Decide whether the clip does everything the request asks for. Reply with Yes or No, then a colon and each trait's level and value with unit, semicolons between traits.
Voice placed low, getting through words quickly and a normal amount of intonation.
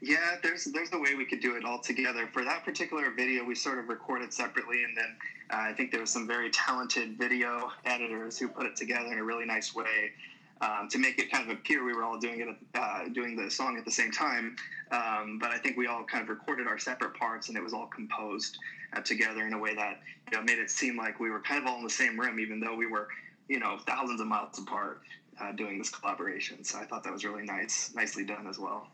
No: low, 115 Hz; fast, 260 wpm; narrow, 1.9 semitones